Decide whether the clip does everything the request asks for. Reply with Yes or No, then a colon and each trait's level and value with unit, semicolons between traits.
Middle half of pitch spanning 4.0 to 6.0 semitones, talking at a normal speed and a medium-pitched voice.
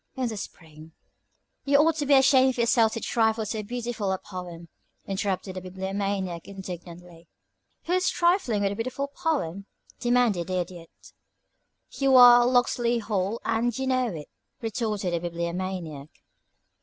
No: average, 5.2 semitones; average, 150 wpm; high, 210 Hz